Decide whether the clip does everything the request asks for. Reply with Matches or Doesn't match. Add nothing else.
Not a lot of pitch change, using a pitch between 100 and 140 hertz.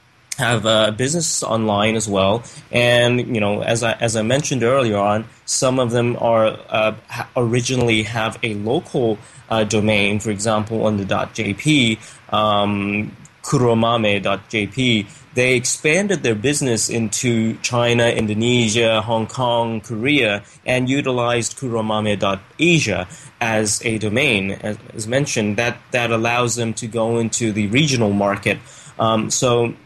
Matches